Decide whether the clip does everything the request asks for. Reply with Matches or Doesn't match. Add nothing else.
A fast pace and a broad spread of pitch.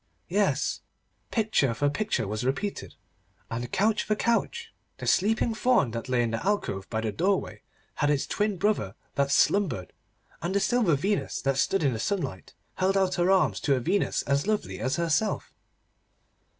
Doesn't match